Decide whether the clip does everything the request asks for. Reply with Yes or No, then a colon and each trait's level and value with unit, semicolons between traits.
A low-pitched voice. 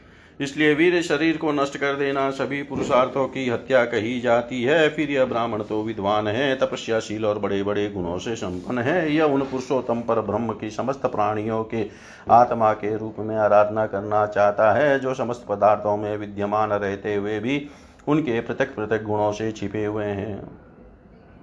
Yes: low, 110 Hz